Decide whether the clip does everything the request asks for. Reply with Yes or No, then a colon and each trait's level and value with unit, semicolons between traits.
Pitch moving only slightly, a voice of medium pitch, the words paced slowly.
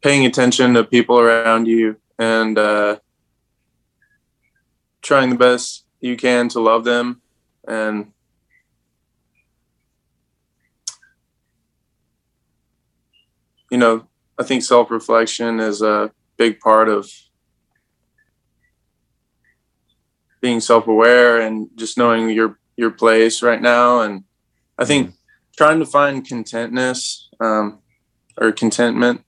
No: narrow, 1.7 semitones; low, 115 Hz; slow, 100 wpm